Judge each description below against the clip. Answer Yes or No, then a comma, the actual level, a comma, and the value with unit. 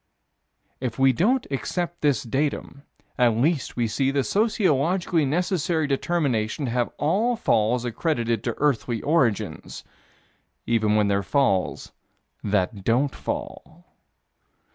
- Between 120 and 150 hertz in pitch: Yes, low, 135 Hz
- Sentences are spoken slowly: Yes, slow, 120 wpm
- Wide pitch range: Yes, wide, 6.4 semitones